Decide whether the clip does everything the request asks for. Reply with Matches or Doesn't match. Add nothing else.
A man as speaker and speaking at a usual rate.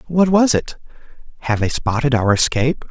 Matches